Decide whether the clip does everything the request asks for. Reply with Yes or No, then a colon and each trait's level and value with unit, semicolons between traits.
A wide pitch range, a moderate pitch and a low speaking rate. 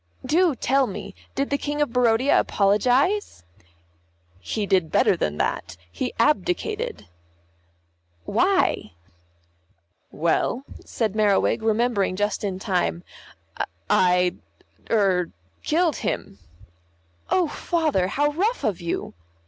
No: wide, 7.5 semitones; high, 225 Hz; slow, 105 wpm